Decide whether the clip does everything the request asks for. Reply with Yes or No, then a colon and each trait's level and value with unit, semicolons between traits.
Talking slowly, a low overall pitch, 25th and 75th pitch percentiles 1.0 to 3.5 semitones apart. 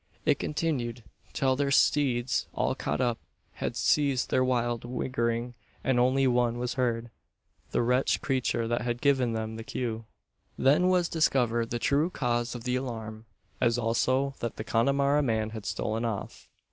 No: average, 160 wpm; low, 120 Hz; narrow, 2.4 semitones